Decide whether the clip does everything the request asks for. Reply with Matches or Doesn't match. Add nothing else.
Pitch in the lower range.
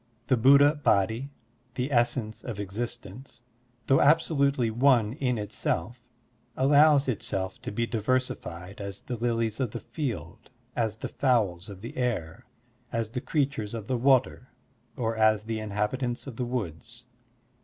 Matches